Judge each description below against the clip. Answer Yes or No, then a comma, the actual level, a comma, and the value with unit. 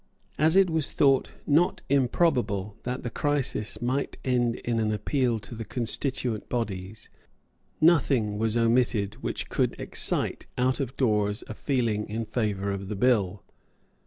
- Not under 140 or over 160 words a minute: Yes, average, 145 wpm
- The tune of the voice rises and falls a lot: No, average, 4.0 semitones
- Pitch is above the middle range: No, low, 120 Hz